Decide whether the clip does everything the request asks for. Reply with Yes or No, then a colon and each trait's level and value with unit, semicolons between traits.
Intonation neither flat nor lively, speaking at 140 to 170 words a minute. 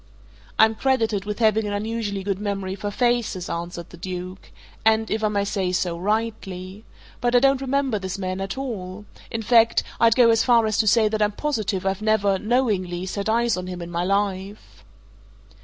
No: average, 3.1 semitones; average, 190 wpm